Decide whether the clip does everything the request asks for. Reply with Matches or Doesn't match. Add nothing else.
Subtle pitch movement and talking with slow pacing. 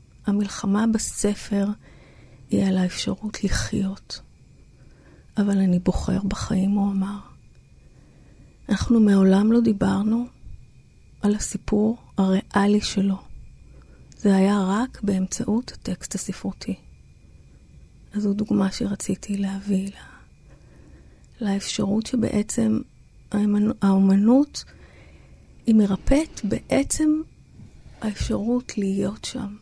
Matches